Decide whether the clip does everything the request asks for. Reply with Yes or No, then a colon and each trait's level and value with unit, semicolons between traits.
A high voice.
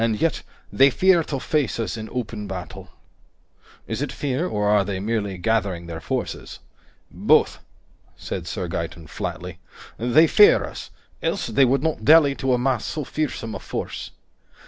No: low, 120 Hz